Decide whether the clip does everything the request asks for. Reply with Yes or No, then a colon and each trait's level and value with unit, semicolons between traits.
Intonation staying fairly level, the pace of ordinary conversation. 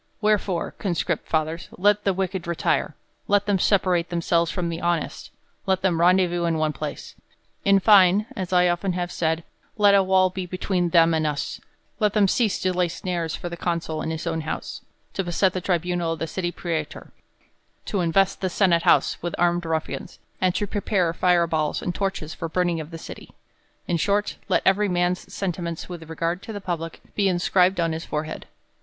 Yes: narrow, 2.2 semitones; average, 190 wpm